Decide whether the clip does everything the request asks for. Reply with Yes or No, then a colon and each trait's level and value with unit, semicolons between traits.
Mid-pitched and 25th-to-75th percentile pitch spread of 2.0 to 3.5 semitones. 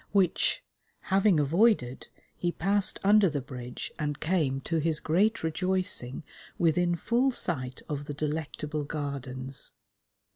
No: medium, 160 Hz; average, 4.9 semitones